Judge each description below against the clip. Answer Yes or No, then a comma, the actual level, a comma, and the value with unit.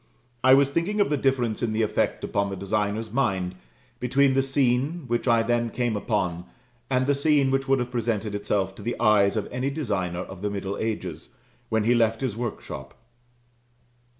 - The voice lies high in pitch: No, low, 115 Hz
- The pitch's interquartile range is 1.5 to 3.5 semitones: No, average, 4.6 semitones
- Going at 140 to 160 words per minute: No, average, 185 wpm